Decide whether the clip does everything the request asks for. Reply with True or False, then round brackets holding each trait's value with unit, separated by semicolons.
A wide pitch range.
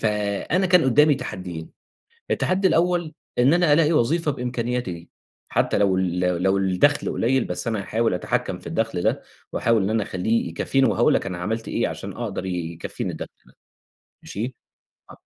True (7.6 semitones)